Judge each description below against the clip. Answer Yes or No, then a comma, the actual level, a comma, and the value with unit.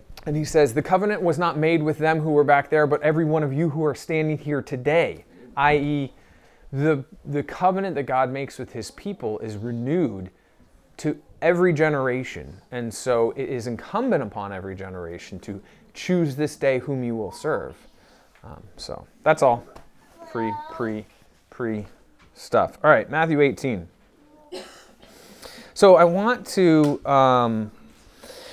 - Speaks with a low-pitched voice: No, medium, 145 Hz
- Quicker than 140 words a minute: Yes, average, 150 wpm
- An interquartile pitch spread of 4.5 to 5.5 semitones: Yes, average, 5.0 semitones